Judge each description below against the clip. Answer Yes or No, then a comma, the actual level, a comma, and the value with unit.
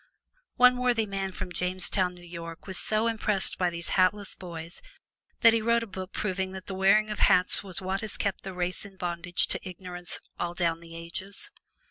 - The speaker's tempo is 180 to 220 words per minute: Yes, average, 195 wpm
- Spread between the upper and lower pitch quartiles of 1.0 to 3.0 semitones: Yes, narrow, 2.5 semitones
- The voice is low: No, medium, 185 Hz